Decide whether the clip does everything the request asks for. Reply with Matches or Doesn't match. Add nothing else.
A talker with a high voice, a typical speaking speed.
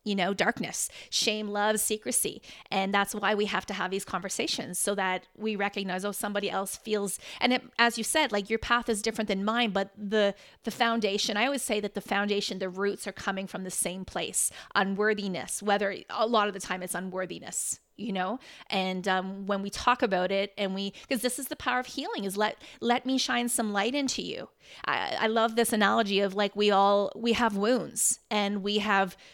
Doesn't match